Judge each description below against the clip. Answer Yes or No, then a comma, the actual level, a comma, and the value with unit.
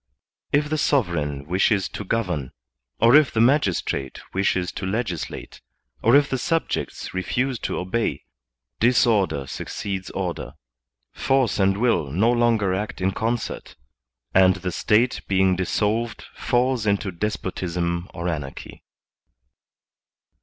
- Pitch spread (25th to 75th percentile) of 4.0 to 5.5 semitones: Yes, average, 4.5 semitones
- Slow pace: Yes, slow, 125 wpm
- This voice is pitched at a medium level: No, low, 100 Hz